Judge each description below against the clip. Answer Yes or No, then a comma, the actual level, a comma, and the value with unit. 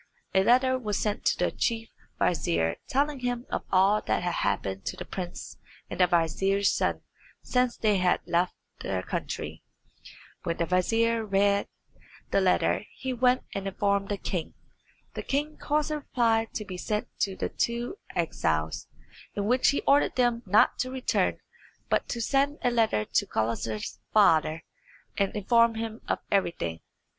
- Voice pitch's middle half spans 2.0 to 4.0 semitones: No, average, 5.2 semitones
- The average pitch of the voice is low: No, high, 210 Hz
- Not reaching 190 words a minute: Yes, average, 160 wpm